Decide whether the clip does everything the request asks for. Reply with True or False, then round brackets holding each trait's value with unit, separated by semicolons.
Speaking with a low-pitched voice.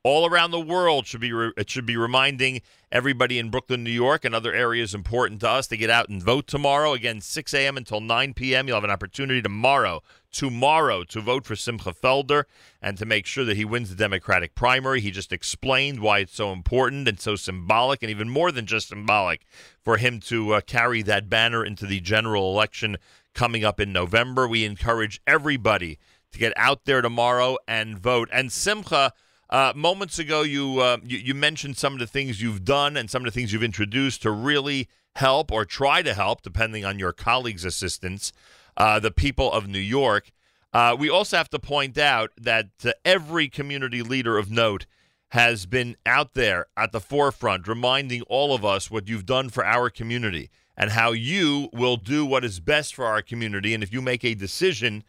True (120 Hz)